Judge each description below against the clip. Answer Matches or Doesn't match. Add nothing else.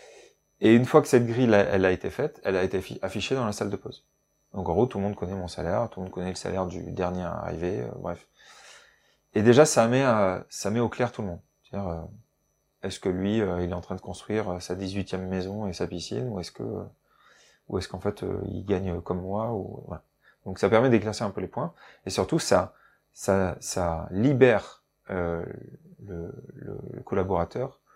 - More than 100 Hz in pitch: Doesn't match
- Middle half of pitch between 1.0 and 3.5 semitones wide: Doesn't match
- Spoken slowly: Doesn't match